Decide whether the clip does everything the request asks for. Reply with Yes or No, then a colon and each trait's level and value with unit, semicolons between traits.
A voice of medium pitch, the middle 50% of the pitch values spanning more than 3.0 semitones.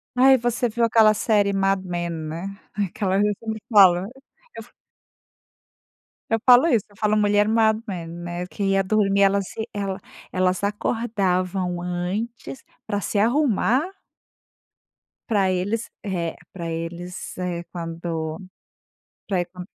No: high, 195 Hz; average, 3.4 semitones